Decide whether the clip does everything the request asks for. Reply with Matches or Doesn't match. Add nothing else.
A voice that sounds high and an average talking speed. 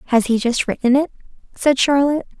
Matches